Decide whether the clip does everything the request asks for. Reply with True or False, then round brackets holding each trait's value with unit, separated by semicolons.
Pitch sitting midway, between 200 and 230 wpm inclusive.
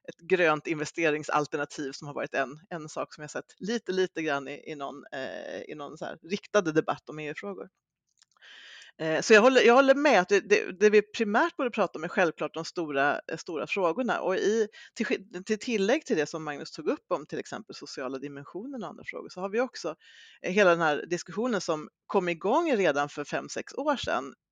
True (175 Hz; 205 wpm)